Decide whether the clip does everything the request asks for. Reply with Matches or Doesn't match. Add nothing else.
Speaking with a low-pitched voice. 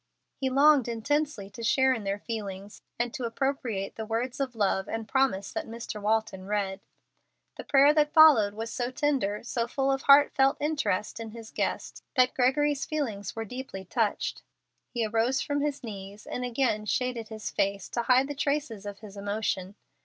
Doesn't match